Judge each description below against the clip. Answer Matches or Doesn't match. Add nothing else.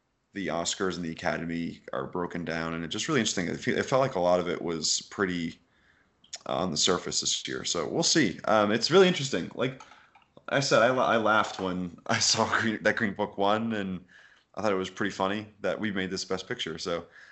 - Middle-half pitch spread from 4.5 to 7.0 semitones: Doesn't match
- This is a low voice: Matches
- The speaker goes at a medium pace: Doesn't match